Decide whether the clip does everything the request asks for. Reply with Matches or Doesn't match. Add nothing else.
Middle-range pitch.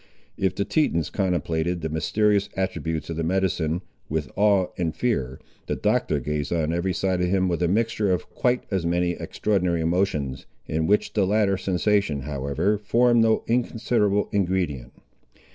Doesn't match